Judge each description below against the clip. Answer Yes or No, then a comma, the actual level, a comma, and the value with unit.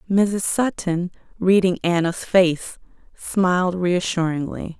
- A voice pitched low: No, medium, 180 Hz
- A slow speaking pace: Yes, slow, 90 wpm